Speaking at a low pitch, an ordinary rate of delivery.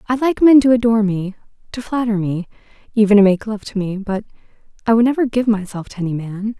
No: high, 215 Hz; average, 190 wpm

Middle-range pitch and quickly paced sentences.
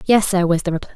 Yes: medium, 180 Hz; fast, 315 wpm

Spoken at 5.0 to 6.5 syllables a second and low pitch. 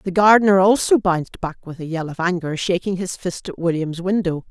No: 5.4 syllables/s; medium, 180 Hz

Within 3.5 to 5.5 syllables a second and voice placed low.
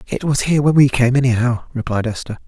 No: 6.5 syllables/s; low, 125 Hz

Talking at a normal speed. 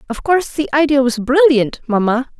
Yes: average, 175 wpm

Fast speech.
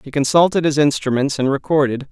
No: average, 170 wpm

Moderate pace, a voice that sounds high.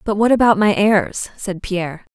Yes: average, 195 wpm; high, 205 Hz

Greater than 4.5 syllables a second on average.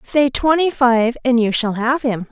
No: 4.2 syllables/s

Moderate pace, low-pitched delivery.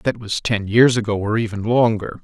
No: fast, 215 wpm; low, 110 Hz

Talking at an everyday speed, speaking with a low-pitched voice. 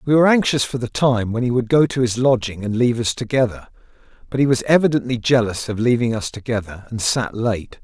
No: fast, 220 wpm; low, 120 Hz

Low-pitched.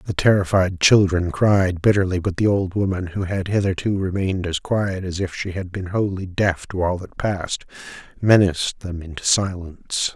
Yes: very low, 95 Hz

